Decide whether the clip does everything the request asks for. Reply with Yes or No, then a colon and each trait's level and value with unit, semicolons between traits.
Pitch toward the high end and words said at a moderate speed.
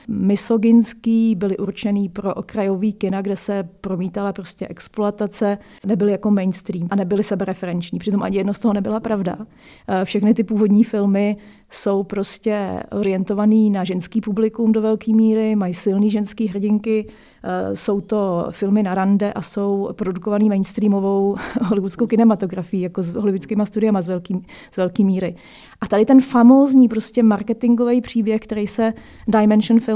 Yes: high, 205 Hz; average, 140 wpm